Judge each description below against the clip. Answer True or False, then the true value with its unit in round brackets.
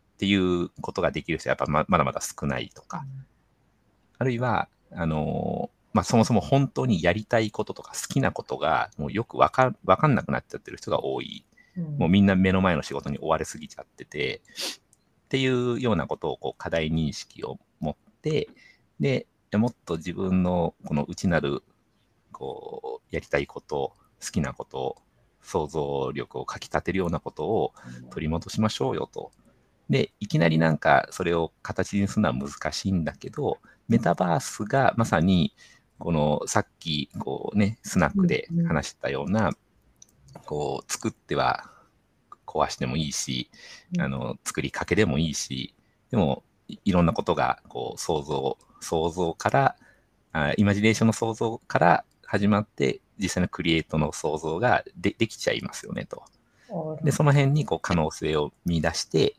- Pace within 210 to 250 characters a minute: False (320 characters per minute)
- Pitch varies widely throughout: True (6.3 semitones)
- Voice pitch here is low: True (95 Hz)